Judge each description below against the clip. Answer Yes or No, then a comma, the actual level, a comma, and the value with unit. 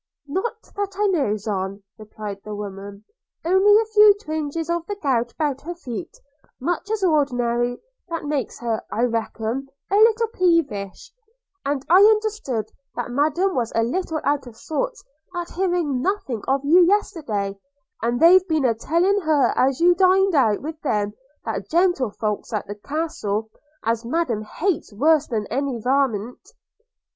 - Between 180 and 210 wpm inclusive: No, average, 160 wpm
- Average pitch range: No, wide, 7.5 semitones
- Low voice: No, very high, 280 Hz